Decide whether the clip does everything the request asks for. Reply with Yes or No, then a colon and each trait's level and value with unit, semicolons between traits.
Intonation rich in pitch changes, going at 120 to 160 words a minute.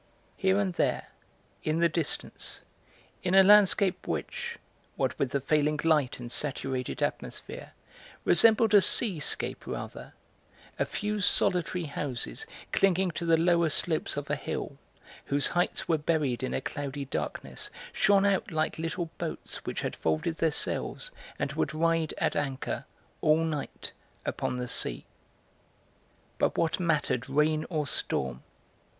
No: average, 4.0 semitones; average, 140 wpm